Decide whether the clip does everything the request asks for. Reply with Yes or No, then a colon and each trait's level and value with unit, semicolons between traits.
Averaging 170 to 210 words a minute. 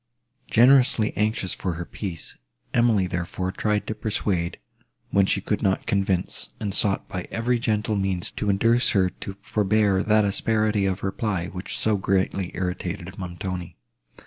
No: average, 145 wpm